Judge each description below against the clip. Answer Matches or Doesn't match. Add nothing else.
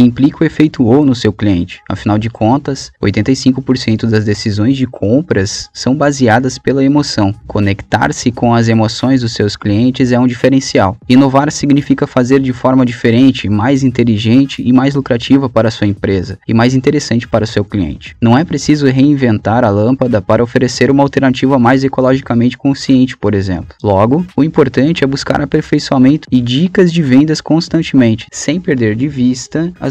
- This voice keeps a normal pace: Matches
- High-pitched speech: Doesn't match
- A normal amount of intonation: Matches